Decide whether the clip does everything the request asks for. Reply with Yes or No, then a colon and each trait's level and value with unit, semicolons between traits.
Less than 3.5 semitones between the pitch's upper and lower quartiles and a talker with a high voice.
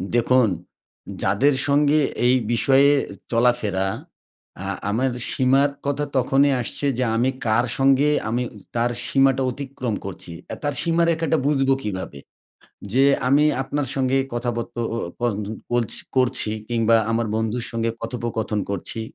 No: average, 3.1 semitones; low, 125 Hz